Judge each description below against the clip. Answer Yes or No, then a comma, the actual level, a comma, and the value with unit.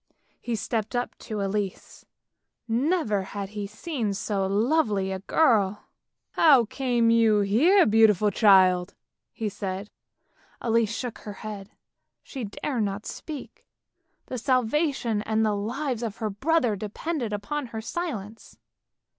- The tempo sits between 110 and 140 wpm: Yes, slow, 135 wpm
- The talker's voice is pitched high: Yes, high, 220 Hz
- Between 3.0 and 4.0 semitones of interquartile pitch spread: Yes, average, 3.7 semitones